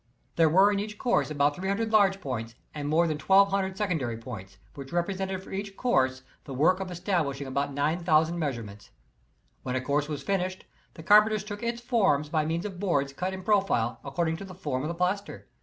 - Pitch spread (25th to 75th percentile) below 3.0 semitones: No, wide, 5.5 semitones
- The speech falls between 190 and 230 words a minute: Yes, average, 195 wpm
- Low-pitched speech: No, medium, 170 Hz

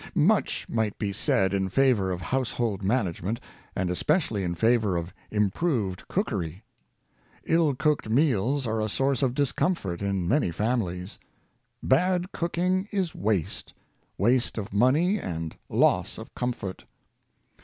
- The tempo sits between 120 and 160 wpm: Yes, average, 140 wpm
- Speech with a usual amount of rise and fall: No, wide, 7.1 semitones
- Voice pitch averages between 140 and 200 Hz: No, low, 115 Hz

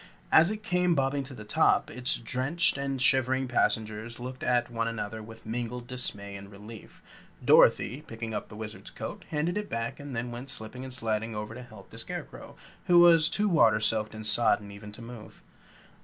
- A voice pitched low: Yes, low, 120 Hz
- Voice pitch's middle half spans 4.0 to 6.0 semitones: No, average, 3.4 semitones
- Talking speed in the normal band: Yes, average, 190 wpm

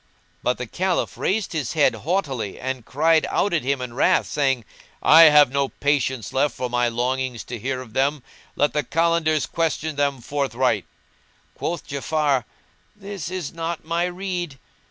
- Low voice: No, medium, 145 Hz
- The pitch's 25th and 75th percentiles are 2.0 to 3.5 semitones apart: No, average, 4.2 semitones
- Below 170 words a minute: Yes, average, 160 wpm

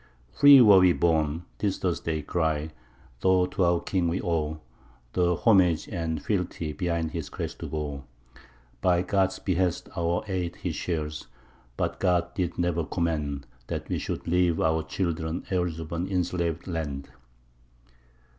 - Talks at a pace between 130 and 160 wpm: Yes, average, 155 wpm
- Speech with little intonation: Yes, narrow, 2.2 semitones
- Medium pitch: No, very low, 85 Hz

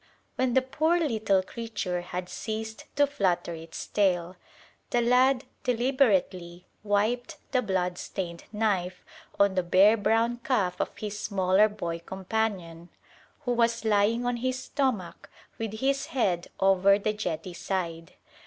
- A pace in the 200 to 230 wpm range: No, slow, 135 wpm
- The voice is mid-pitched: No, high, 210 Hz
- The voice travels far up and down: No, average, 4.7 semitones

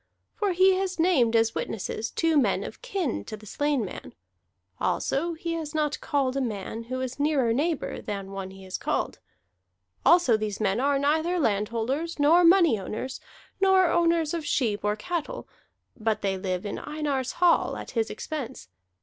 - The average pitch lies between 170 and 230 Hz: No, very high, 275 Hz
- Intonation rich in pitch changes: Yes, wide, 7.3 semitones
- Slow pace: No, average, 170 wpm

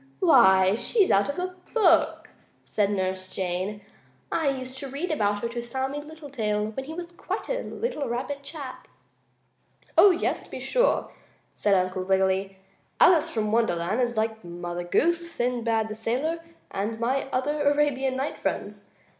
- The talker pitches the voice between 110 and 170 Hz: No, high, 240 Hz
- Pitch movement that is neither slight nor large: No, wide, 6.3 semitones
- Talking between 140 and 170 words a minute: Yes, average, 155 wpm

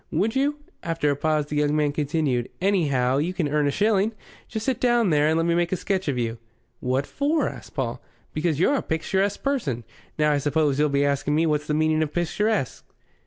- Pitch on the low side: No, medium, 155 Hz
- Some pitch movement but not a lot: Yes, average, 4.8 semitones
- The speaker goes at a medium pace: No, fast, 215 wpm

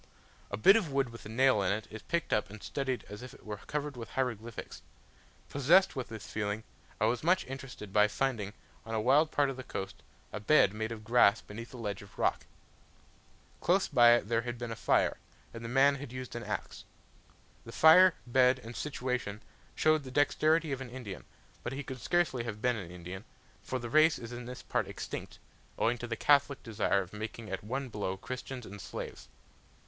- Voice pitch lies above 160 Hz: No, low, 120 Hz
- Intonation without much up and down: No, average, 4.0 semitones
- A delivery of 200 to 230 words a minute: Yes, fast, 205 wpm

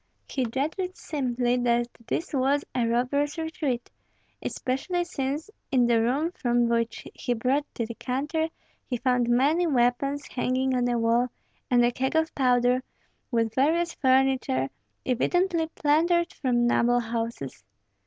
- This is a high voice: Yes, very high, 255 Hz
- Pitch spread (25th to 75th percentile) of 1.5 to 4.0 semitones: Yes, average, 3.4 semitones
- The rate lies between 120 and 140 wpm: Yes, slow, 135 wpm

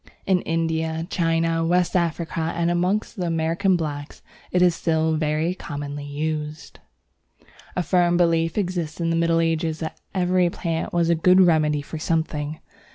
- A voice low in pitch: No, medium, 165 Hz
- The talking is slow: No, average, 155 wpm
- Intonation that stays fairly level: Yes, narrow, 1.6 semitones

